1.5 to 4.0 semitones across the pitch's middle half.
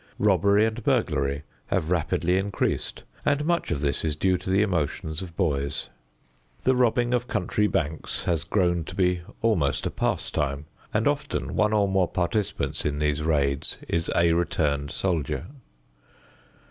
No: average, 5.1 semitones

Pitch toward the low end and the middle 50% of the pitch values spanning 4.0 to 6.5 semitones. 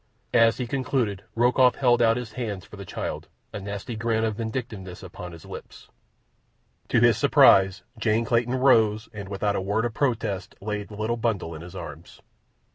No: low, 110 Hz; average, 3.3 semitones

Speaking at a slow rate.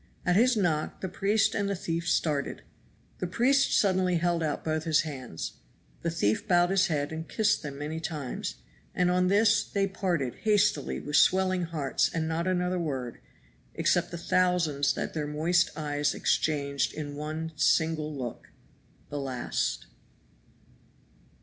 No: average, 150 wpm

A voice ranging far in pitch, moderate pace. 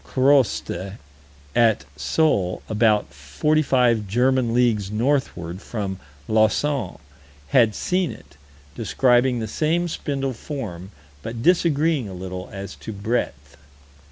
No: wide, 5.7 semitones; slow, 110 wpm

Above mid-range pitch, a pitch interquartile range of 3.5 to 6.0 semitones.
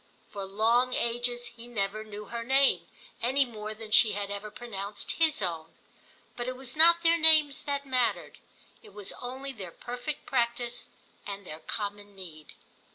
Yes: high, 235 Hz; average, 4.2 semitones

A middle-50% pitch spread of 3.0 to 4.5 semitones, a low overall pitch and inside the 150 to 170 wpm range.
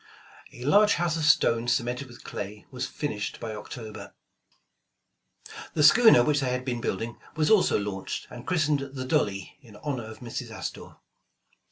No: average, 5.1 semitones; low, 125 Hz; average, 165 wpm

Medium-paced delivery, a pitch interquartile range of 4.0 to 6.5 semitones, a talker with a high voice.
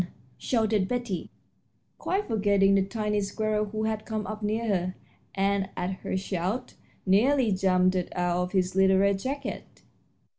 No: average, 145 wpm; narrow, 2.4 semitones; high, 200 Hz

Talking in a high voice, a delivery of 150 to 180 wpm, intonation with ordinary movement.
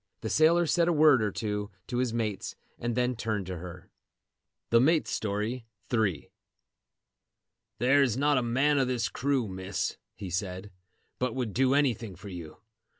No: low, 115 Hz; average, 160 wpm; average, 4.5 semitones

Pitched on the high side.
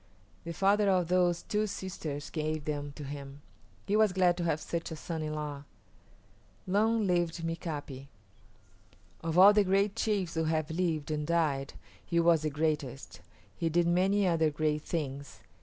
No: medium, 165 Hz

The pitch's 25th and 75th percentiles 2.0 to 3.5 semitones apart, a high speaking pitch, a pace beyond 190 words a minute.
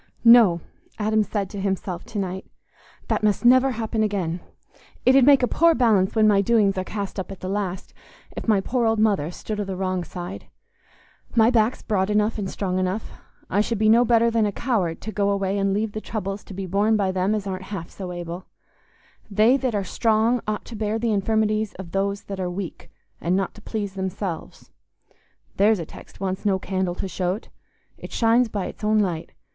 Yes: narrow, 2.5 semitones; high, 205 Hz; fast, 205 wpm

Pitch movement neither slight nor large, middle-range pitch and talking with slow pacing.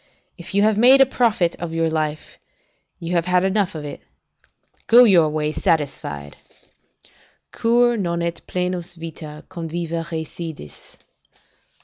Yes: average, 3.3 semitones; medium, 170 Hz; slow, 125 wpm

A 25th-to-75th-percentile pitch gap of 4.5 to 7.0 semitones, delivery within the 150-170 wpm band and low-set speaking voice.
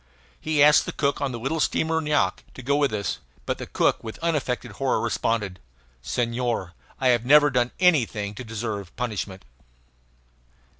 Yes: average, 4.9 semitones; average, 160 wpm; low, 125 Hz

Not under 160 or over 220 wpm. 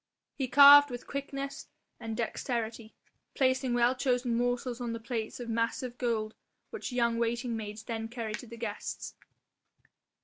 No: average, 145 wpm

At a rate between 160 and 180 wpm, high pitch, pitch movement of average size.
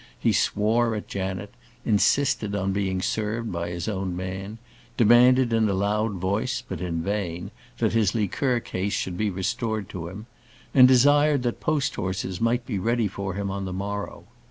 No: average, 175 wpm; low, 100 Hz; average, 3.7 semitones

